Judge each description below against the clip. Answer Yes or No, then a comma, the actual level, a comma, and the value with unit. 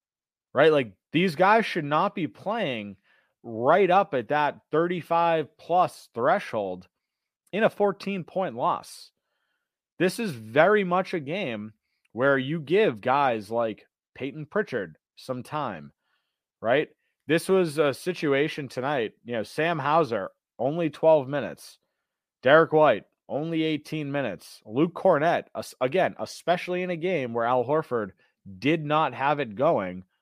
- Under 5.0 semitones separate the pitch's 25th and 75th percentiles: No, wide, 5.4 semitones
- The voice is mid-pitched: Yes, medium, 155 Hz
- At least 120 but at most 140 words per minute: Yes, slow, 135 wpm